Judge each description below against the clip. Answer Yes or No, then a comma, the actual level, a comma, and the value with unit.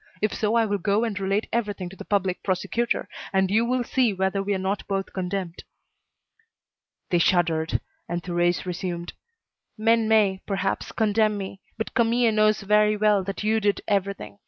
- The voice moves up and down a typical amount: No, narrow, 2.3 semitones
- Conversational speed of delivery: Yes, average, 170 wpm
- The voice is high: Yes, high, 200 Hz